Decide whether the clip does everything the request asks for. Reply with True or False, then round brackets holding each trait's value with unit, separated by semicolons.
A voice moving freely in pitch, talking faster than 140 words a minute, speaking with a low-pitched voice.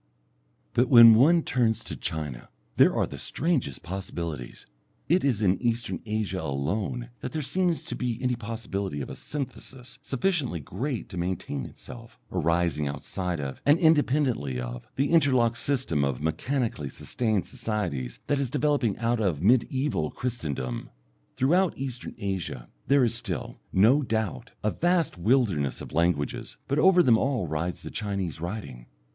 True (7.7 semitones; 150 wpm; 110 Hz)